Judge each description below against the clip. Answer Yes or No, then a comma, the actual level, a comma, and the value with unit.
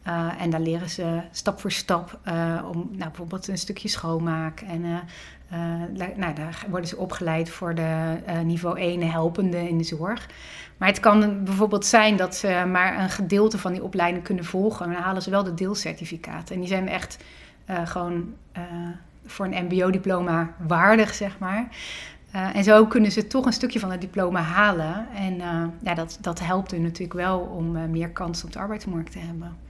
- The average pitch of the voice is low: No, medium, 180 Hz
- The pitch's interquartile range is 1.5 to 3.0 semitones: Yes, average, 2.7 semitones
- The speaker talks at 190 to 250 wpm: Yes, average, 195 wpm